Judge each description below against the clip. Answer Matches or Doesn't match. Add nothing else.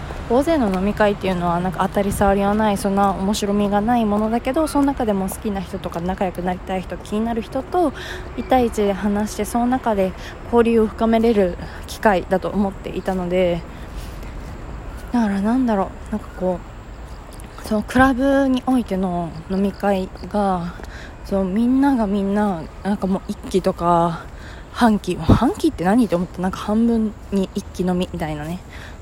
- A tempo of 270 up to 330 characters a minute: Matches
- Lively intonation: Doesn't match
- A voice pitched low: Doesn't match